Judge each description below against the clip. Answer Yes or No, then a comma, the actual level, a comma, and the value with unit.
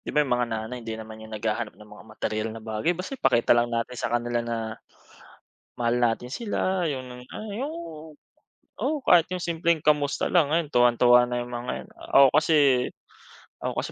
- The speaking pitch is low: Yes, low, 120 Hz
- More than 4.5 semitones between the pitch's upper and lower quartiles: Yes, average, 5.1 semitones